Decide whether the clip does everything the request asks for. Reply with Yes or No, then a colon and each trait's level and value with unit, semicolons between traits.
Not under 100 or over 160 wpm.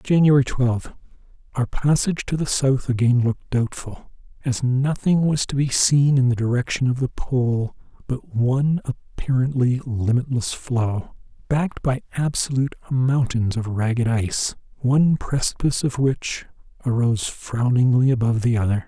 Yes: slow, 135 wpm